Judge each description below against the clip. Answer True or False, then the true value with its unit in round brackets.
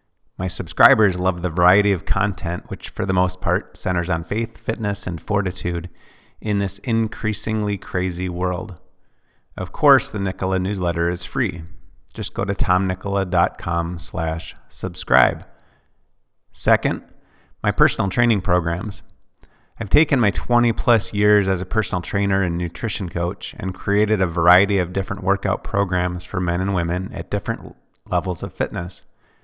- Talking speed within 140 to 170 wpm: True (145 wpm)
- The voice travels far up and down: False (2.6 semitones)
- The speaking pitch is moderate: False (95 Hz)